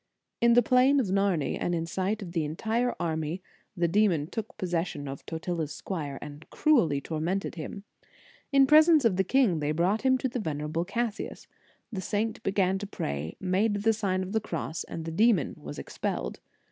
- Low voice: No, medium, 185 Hz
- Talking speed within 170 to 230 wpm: Yes, average, 190 wpm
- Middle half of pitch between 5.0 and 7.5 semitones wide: Yes, wide, 5.5 semitones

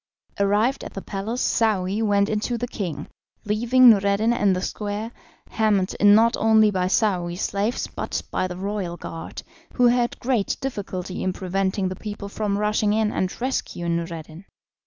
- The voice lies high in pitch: Yes, high, 205 Hz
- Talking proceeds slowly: No, average, 165 wpm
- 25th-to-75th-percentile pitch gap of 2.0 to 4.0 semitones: Yes, average, 2.8 semitones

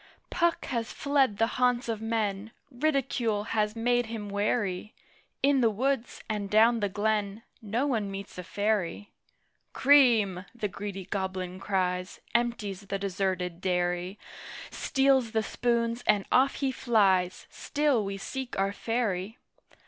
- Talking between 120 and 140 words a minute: Yes, slow, 135 wpm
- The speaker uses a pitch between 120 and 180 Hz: No, high, 215 Hz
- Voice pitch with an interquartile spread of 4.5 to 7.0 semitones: No, average, 3.6 semitones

